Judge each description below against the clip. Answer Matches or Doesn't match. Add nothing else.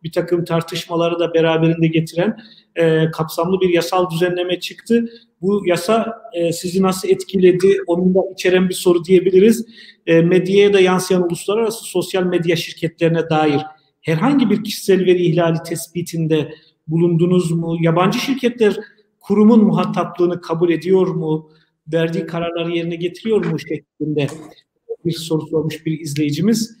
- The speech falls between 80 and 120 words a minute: Doesn't match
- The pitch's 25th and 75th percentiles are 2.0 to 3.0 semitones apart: Matches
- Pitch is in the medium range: Matches